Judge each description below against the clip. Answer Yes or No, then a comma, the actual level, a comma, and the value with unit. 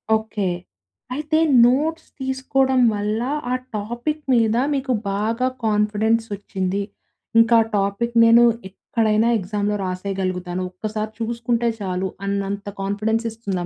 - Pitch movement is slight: No, average, 3.0 semitones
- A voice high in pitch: Yes, high, 220 Hz